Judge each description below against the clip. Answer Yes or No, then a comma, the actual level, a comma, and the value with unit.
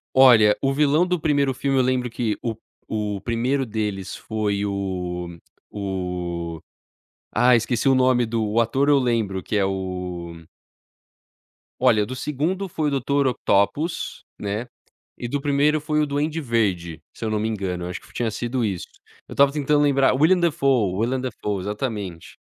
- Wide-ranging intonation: Yes, wide, 5.7 semitones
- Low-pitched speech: Yes, low, 115 Hz